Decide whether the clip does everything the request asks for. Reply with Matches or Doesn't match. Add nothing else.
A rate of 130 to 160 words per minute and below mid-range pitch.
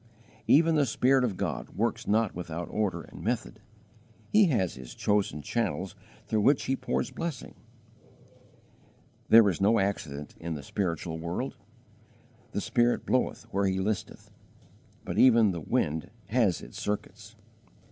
Matches